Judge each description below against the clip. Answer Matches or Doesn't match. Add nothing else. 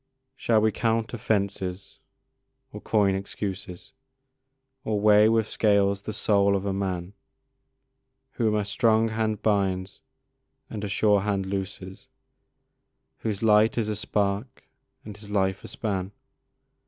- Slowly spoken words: Matches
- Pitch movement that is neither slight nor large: Doesn't match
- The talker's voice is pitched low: Matches